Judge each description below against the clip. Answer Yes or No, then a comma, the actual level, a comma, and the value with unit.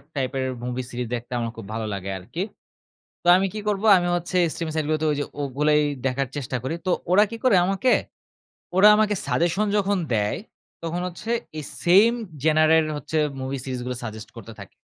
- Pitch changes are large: Yes, wide, 6.5 semitones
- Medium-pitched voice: Yes, medium, 155 Hz